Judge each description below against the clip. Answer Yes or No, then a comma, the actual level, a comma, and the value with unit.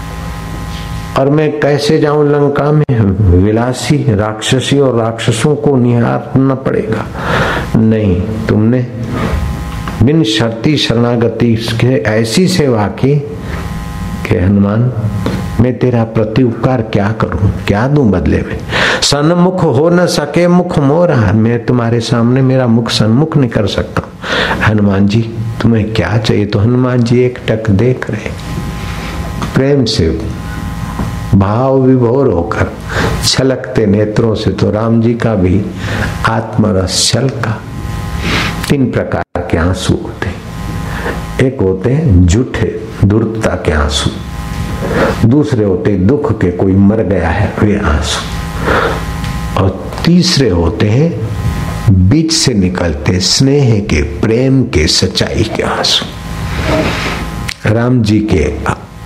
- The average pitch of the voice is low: Yes, low, 110 Hz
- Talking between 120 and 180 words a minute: No, slow, 110 wpm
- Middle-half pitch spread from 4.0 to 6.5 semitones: Yes, average, 5.0 semitones